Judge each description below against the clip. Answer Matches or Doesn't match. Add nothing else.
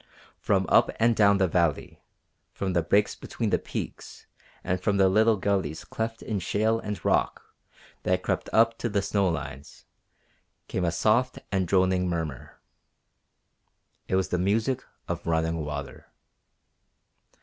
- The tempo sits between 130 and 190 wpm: Matches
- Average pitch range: Matches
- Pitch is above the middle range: Doesn't match